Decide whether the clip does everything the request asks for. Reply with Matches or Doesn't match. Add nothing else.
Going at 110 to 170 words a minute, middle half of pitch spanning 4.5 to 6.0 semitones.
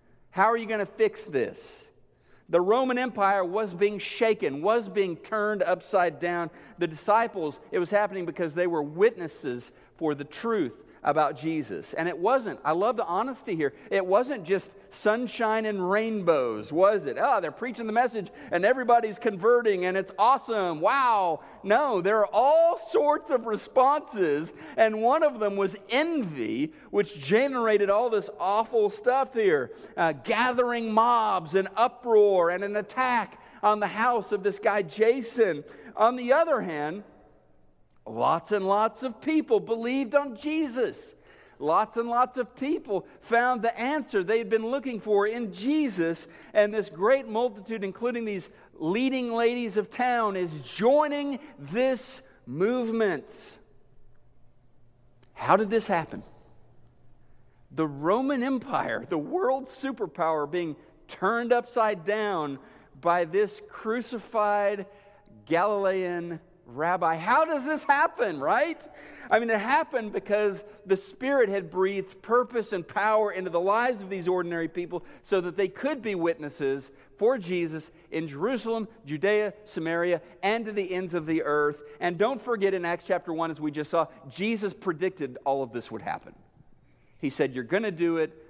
Matches